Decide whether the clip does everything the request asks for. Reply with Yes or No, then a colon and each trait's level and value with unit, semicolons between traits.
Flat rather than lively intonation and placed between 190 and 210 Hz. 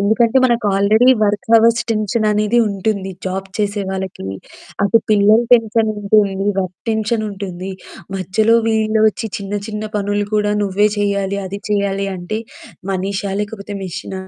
Yes: narrow, 1.9 semitones; high, 205 Hz